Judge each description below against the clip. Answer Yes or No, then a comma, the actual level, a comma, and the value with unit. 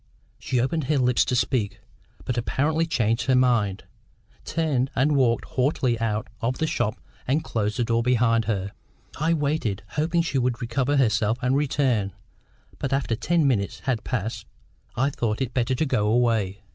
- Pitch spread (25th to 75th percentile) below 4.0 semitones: Yes, average, 3.4 semitones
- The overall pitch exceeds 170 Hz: No, low, 125 Hz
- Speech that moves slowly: No, average, 170 wpm